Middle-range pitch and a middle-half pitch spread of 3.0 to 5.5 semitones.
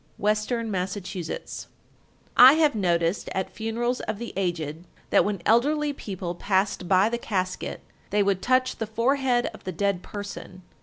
No: high, 205 Hz; average, 4.3 semitones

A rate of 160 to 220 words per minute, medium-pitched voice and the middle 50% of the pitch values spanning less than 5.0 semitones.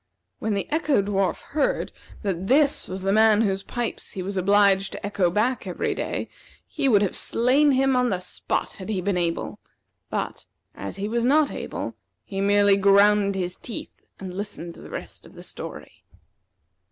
No: average, 180 wpm; high, 200 Hz; average, 3.7 semitones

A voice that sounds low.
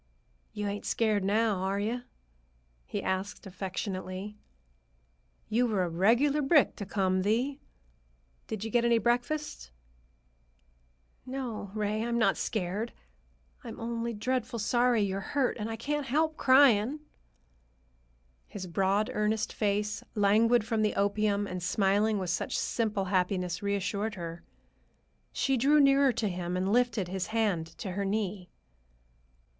No: high, 210 Hz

